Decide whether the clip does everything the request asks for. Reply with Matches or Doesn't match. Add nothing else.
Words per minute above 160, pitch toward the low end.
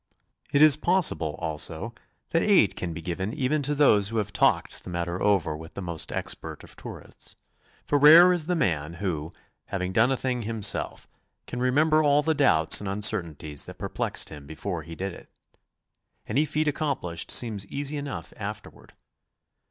Matches